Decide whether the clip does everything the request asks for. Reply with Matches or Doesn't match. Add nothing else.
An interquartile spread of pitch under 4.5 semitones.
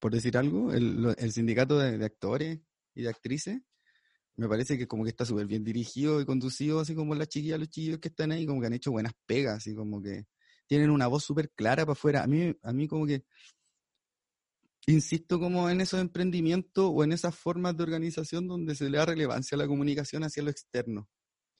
Doesn't match